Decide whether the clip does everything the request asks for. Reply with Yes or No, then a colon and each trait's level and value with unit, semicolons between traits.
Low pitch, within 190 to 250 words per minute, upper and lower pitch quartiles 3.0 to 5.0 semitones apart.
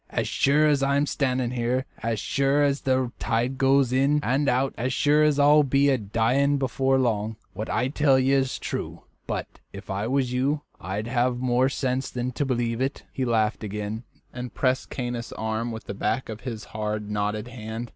Yes: low, 125 Hz; average, 195 wpm; average, 3.3 semitones